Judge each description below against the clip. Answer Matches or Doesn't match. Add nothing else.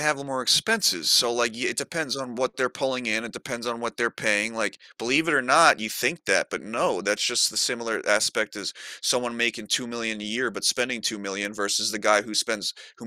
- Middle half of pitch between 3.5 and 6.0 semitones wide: Doesn't match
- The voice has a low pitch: Matches